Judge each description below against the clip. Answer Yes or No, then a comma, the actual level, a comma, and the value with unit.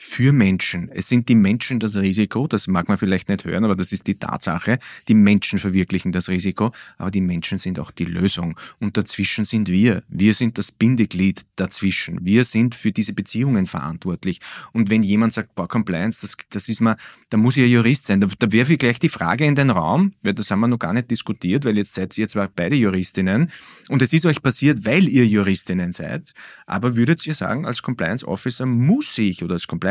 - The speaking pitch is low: Yes, low, 110 Hz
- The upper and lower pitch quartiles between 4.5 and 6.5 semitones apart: No, average, 4.1 semitones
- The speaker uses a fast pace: Yes, fast, 215 wpm